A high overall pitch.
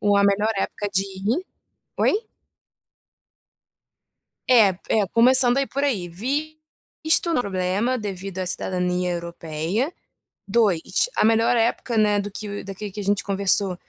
Yes: high, 205 Hz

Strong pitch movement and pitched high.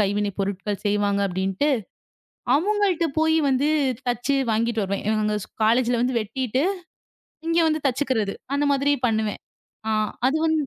Yes: wide, 5.8 semitones; high, 240 Hz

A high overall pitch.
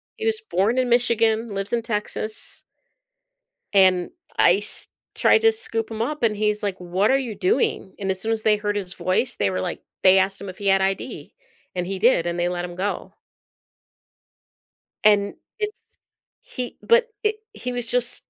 Yes: high, 210 Hz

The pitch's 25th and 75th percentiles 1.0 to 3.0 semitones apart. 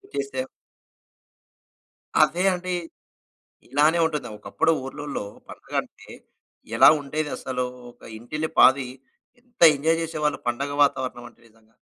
No: average, 3.5 semitones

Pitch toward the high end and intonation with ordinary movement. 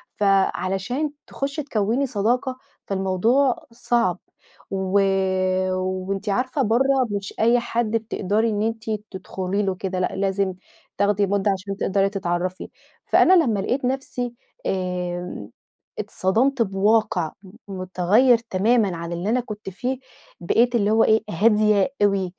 Yes: high, 205 Hz; average, 3.9 semitones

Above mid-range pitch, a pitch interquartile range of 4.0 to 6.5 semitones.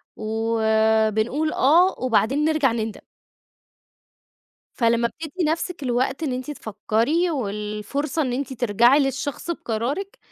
Yes: very high, 255 Hz; average, 5.2 semitones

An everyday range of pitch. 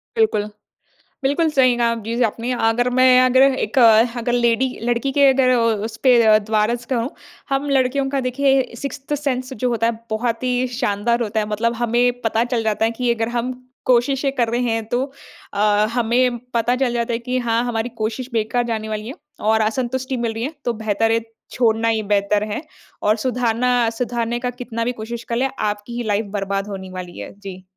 No: narrow, 2.2 semitones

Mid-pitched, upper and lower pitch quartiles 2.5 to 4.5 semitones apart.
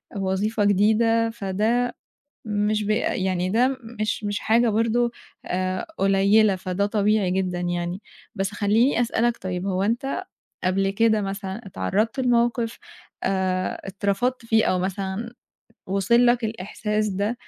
No: high, 205 Hz; average, 3.1 semitones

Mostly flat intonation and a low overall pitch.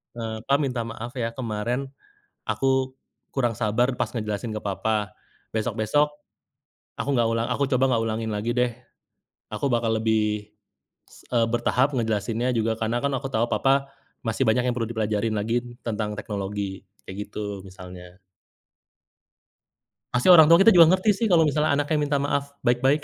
No: average, 3.8 semitones; low, 115 Hz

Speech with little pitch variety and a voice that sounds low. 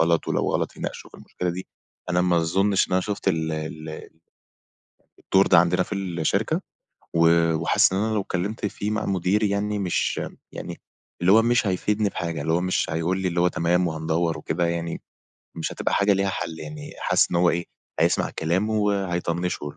No: average, 3.0 semitones; very low, 90 Hz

